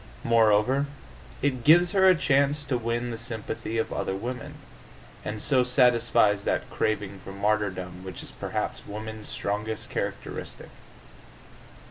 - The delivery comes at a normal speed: No, slow, 130 wpm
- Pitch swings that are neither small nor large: Yes, average, 3.7 semitones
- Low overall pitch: Yes, low, 115 Hz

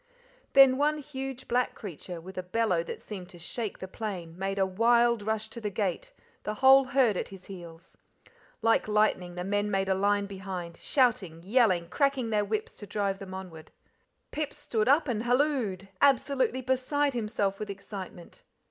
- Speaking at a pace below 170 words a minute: No, average, 175 wpm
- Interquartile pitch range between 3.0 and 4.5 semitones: No, average, 4.9 semitones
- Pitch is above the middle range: Yes, high, 210 Hz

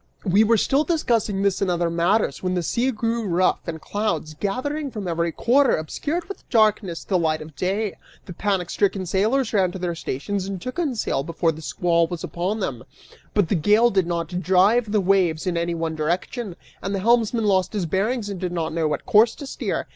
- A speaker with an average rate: No, fast, 210 wpm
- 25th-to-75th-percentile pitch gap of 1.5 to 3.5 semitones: No, average, 4.5 semitones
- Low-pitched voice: No, high, 190 Hz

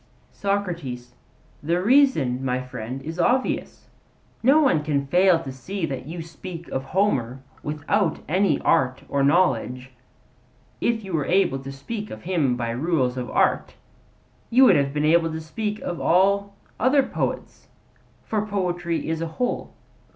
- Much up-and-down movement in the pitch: Yes, wide, 6.5 semitones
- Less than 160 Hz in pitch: No, medium, 165 Hz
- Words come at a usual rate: Yes, average, 150 wpm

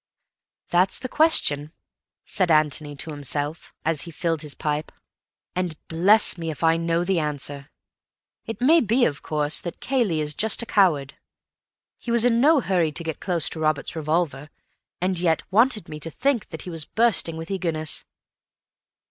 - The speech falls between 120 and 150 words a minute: No, average, 175 wpm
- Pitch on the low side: No, medium, 165 Hz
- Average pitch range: Yes, average, 4.7 semitones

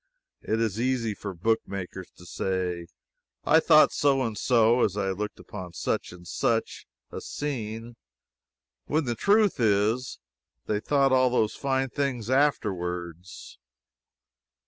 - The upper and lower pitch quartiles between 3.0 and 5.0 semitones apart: No, wide, 5.5 semitones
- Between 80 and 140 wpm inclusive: Yes, slow, 135 wpm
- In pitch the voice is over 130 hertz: No, low, 110 Hz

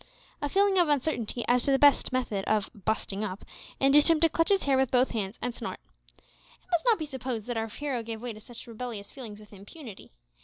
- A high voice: Yes, high, 245 Hz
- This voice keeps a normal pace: No, fast, 225 wpm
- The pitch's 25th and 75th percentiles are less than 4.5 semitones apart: No, average, 5.0 semitones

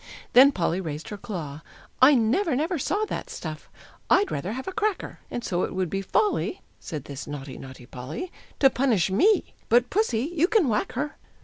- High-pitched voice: Yes, high, 235 Hz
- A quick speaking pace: No, average, 190 wpm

